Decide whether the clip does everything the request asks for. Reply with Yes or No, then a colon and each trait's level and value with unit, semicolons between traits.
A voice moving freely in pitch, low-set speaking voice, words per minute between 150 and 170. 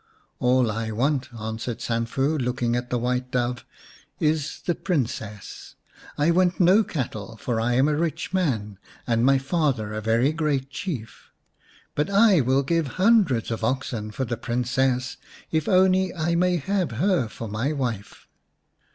Yes: wide, 5.7 semitones; low, 130 Hz; average, 160 wpm